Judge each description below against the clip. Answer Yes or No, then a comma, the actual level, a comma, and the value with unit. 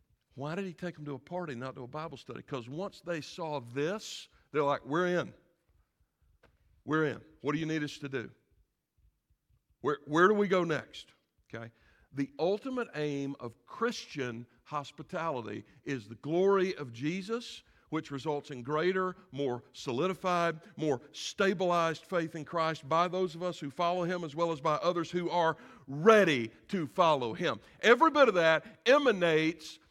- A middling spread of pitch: Yes, average, 4.4 semitones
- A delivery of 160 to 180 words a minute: Yes, average, 165 wpm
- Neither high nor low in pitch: Yes, medium, 155 Hz